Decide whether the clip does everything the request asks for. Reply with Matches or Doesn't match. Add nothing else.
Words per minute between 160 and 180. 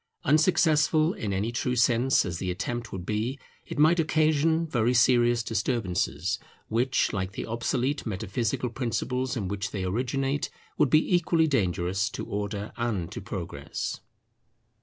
Doesn't match